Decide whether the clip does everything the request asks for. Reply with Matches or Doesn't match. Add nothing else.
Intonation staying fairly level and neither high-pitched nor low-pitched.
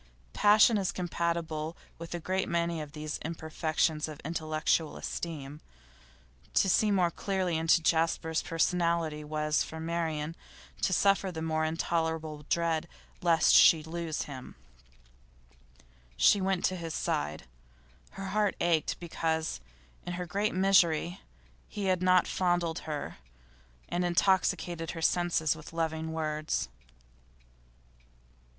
Matches